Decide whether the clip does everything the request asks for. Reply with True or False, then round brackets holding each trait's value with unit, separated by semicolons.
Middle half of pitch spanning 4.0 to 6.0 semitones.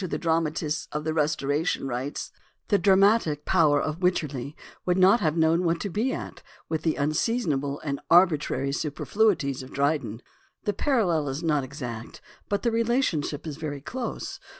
True (4.4 semitones)